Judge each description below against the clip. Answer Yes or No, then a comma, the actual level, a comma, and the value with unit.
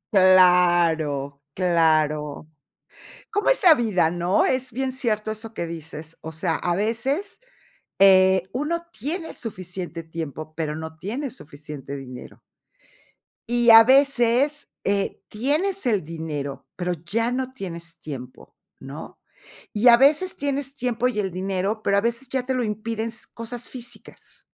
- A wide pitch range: Yes, wide, 7.3 semitones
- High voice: Yes, high, 200 Hz